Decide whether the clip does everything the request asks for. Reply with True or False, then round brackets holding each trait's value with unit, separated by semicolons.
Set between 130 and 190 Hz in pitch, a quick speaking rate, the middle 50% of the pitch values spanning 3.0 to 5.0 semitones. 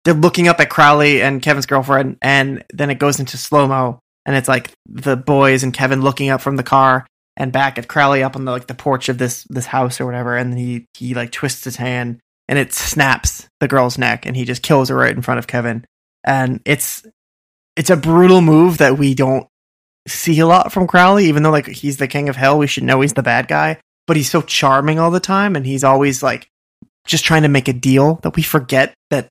False (135 Hz; 235 wpm; 2.6 semitones)